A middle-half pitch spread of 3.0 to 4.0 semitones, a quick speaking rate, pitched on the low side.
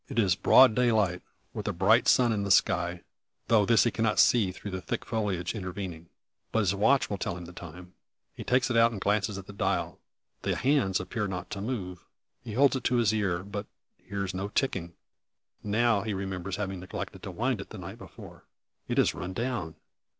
Yes: average, 3.7 semitones; fast, 210 wpm; low, 100 Hz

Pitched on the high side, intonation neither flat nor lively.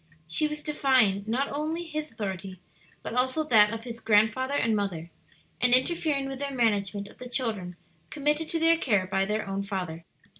No: high, 230 Hz; wide, 6.2 semitones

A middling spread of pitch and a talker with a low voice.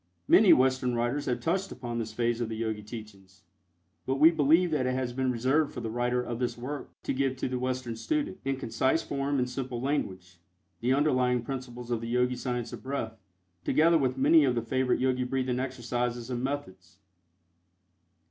No: narrow, 2.2 semitones; low, 125 Hz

